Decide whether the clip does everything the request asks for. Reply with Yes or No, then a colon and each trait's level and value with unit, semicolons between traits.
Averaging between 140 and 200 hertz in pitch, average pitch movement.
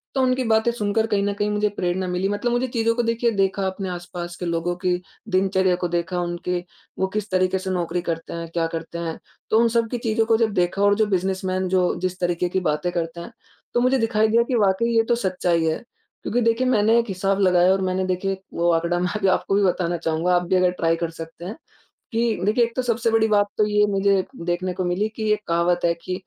Yes: high, 190 Hz; average, 3.6 semitones